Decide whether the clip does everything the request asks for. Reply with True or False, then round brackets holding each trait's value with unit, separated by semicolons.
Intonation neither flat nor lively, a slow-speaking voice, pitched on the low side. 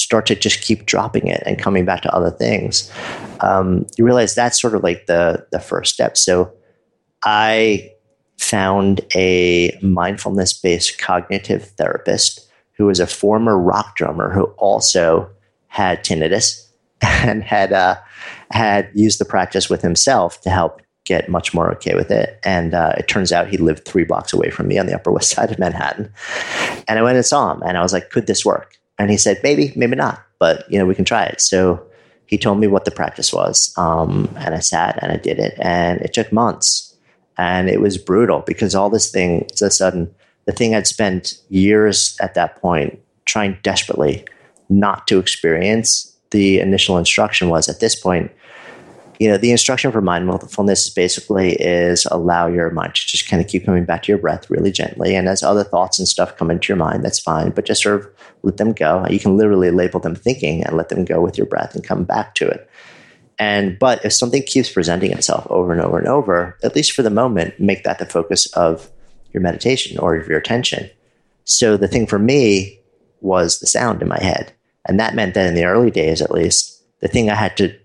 False (3.0 semitones; 205 wpm; 95 Hz)